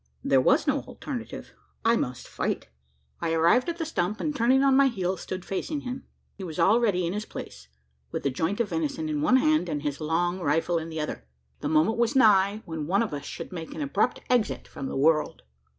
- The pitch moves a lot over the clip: Yes, wide, 6.9 semitones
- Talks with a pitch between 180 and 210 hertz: Yes, medium, 185 Hz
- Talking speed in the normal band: No, fast, 215 wpm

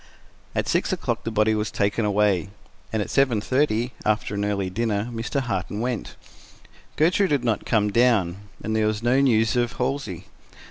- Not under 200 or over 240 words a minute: No, average, 175 wpm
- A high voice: No, low, 110 Hz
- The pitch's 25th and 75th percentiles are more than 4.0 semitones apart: No, average, 3.0 semitones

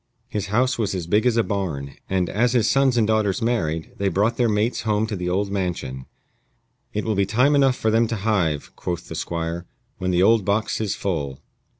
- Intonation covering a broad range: No, average, 4.0 semitones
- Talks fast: Yes, fast, 215 wpm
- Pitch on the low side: Yes, low, 105 Hz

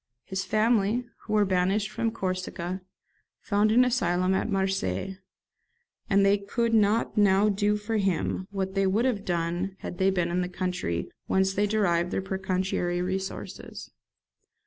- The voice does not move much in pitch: Yes, narrow, 2.2 semitones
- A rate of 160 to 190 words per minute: No, average, 150 wpm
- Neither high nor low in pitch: No, high, 195 Hz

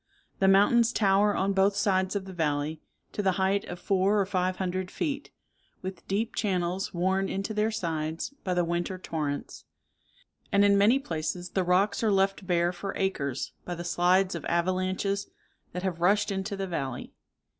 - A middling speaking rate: Yes, average, 175 wpm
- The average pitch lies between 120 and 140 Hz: No, high, 190 Hz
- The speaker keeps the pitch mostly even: Yes, narrow, 2.2 semitones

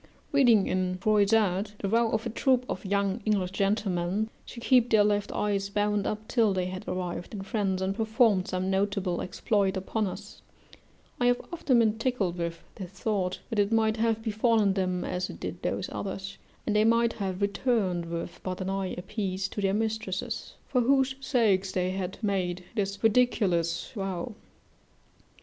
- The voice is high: Yes, high, 200 Hz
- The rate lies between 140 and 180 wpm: Yes, average, 175 wpm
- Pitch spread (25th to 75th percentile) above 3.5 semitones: No, average, 2.9 semitones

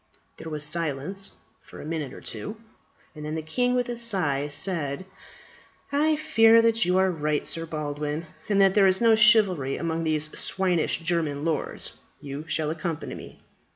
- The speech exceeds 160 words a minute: Yes, average, 170 wpm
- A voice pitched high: No, medium, 165 Hz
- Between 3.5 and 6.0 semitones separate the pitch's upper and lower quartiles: Yes, average, 4.8 semitones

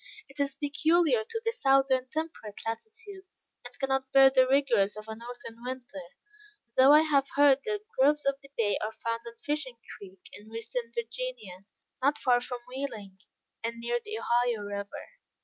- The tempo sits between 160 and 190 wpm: Yes, average, 165 wpm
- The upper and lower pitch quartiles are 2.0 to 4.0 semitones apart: Yes, average, 3.7 semitones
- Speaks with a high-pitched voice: Yes, very high, 255 Hz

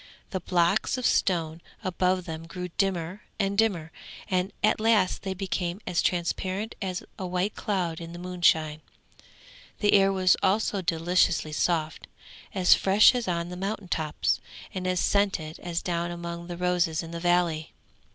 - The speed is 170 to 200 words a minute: No, average, 160 wpm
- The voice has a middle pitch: Yes, medium, 180 Hz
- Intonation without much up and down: Yes, narrow, 2.2 semitones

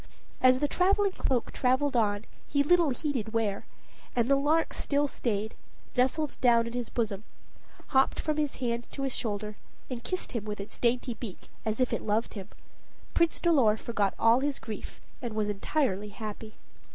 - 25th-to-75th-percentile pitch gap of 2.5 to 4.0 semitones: No, average, 4.6 semitones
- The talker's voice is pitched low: No, high, 240 Hz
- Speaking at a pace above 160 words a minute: Yes, average, 175 wpm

